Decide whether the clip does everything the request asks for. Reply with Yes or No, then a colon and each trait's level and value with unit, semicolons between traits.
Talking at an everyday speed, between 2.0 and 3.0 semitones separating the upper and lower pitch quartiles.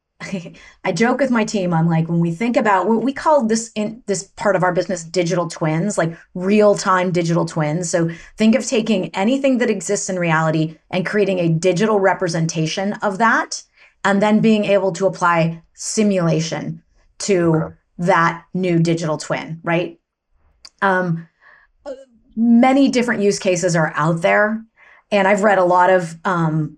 No: average, 160 wpm; average, 4.0 semitones